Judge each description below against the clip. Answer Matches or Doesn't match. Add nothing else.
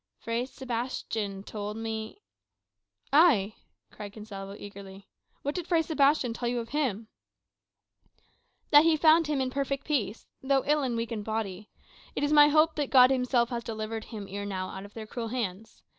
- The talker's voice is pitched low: Doesn't match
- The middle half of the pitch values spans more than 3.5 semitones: Matches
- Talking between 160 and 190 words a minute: Matches